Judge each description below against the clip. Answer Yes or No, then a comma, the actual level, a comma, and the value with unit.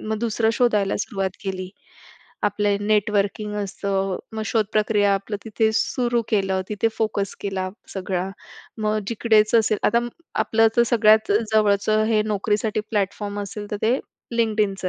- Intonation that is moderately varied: No, narrow, 1.6 semitones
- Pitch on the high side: Yes, high, 210 Hz